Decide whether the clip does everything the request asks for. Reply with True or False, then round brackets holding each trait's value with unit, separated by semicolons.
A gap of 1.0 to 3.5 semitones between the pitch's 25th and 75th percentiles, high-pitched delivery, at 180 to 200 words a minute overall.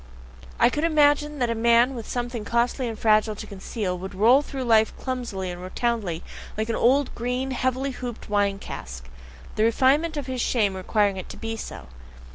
False (3.9 semitones; 235 Hz; 185 wpm)